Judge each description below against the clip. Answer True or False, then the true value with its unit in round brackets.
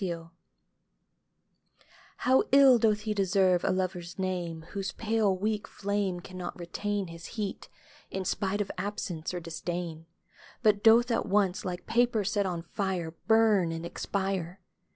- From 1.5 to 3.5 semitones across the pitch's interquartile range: True (3.0 semitones)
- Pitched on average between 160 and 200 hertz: True (190 Hz)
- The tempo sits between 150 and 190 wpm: False (140 wpm)